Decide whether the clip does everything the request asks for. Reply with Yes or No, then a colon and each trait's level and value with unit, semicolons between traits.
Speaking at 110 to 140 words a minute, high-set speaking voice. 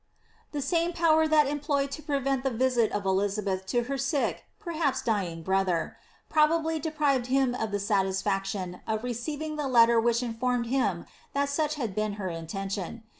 No: average, 175 wpm; high, 245 Hz